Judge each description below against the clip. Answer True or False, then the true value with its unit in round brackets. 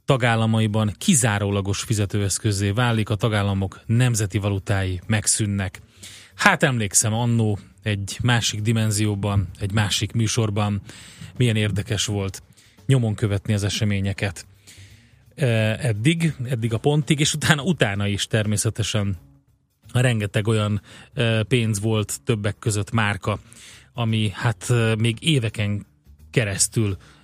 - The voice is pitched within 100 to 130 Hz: True (110 Hz)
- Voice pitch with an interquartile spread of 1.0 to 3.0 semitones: True (2.5 semitones)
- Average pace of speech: False (100 wpm)